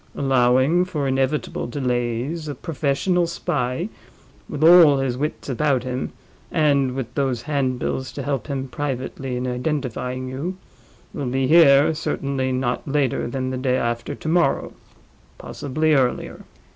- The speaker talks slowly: Yes, slow, 130 wpm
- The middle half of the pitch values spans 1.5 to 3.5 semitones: Yes, average, 2.8 semitones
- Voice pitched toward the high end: No, low, 135 Hz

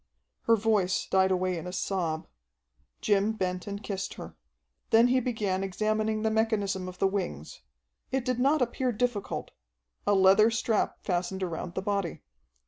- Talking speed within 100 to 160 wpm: Yes, average, 155 wpm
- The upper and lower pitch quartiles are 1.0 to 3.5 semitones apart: Yes, average, 3.1 semitones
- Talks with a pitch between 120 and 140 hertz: No, high, 200 Hz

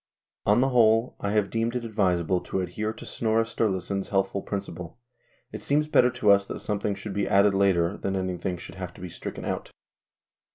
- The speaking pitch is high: No, low, 100 Hz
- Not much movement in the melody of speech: No, average, 3.1 semitones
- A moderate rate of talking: No, fast, 210 wpm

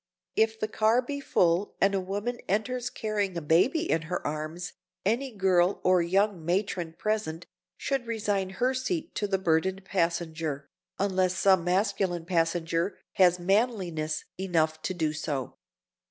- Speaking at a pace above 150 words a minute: No, average, 145 wpm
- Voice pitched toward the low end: No, medium, 185 Hz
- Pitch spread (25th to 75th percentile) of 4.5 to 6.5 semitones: No, average, 4.1 semitones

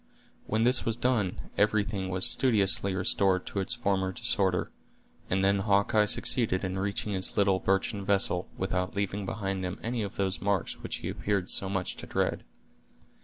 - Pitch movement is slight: Yes, narrow, 1.8 semitones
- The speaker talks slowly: No, average, 170 wpm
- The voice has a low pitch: Yes, low, 100 Hz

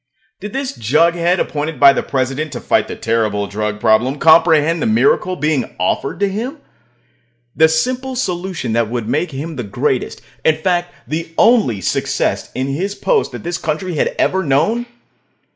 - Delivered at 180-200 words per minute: No, average, 165 wpm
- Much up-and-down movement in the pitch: Yes, wide, 6.1 semitones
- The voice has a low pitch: No, medium, 160 Hz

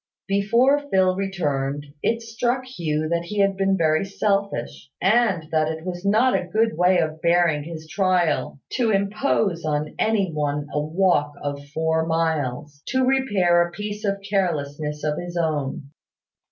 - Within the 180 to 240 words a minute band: No, average, 155 wpm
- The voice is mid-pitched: Yes, medium, 175 Hz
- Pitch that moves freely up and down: No, average, 4.4 semitones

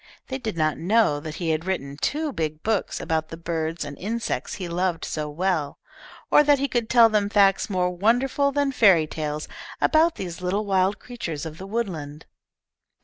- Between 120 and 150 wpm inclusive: No, average, 185 wpm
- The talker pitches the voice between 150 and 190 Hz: Yes, medium, 185 Hz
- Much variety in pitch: Yes, wide, 6.1 semitones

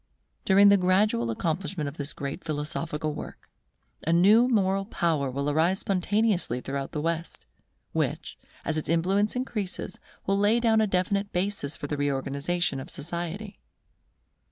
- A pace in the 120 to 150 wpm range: Yes, average, 145 wpm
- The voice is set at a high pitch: No, medium, 175 Hz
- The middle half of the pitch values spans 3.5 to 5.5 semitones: Yes, average, 5.2 semitones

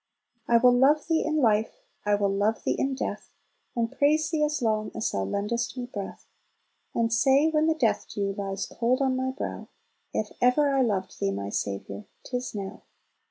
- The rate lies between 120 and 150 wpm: No, average, 190 wpm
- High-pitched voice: Yes, high, 235 Hz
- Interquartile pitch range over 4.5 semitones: Yes, average, 5.1 semitones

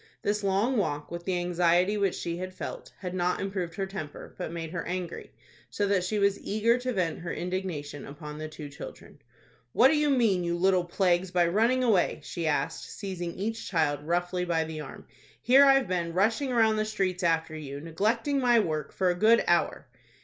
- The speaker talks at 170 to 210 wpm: Yes, average, 200 wpm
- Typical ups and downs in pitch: Yes, average, 3.9 semitones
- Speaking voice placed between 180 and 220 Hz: Yes, medium, 185 Hz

